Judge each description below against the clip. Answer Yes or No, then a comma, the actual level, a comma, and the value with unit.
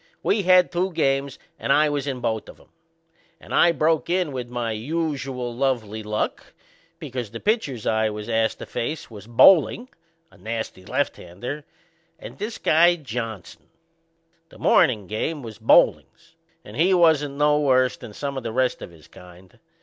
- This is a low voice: Yes, low, 130 Hz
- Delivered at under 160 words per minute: No, average, 165 wpm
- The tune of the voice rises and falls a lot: Yes, wide, 5.8 semitones